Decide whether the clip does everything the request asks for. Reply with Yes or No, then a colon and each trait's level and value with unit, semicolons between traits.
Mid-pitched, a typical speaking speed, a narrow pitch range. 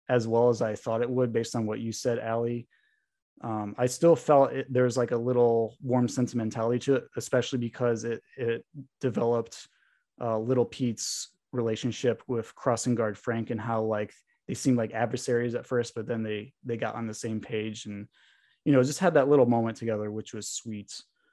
No: low, 120 Hz; average, 195 wpm; narrow, 1.9 semitones